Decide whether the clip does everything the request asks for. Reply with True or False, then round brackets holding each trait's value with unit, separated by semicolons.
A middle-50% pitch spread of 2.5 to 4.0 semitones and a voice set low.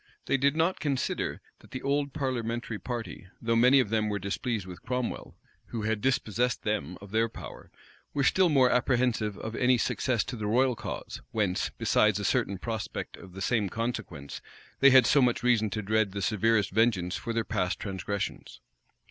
True (3.6 semitones; 115 Hz)